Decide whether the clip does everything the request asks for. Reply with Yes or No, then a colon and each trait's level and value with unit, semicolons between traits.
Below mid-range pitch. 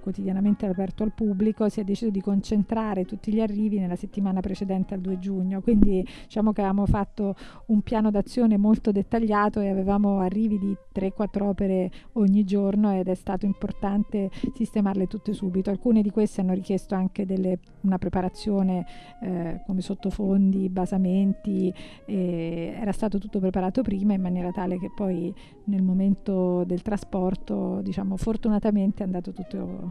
No: high, 195 Hz